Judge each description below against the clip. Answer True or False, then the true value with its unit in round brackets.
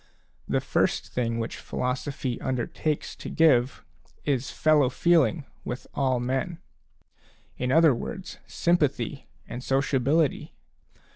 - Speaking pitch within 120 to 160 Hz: True (135 Hz)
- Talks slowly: True (110 wpm)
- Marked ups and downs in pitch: False (3.7 semitones)